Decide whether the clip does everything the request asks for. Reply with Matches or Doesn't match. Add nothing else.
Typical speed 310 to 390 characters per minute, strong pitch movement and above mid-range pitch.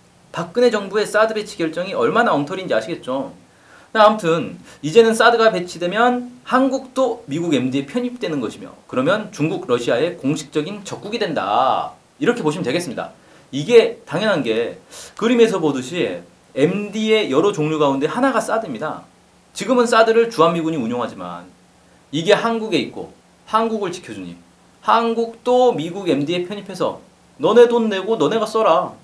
Matches